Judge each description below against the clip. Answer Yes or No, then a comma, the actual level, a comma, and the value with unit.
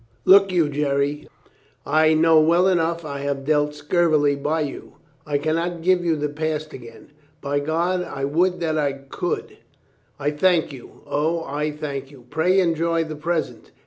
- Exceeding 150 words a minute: Yes, average, 175 wpm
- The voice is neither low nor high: Yes, medium, 155 Hz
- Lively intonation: No, narrow, 2.6 semitones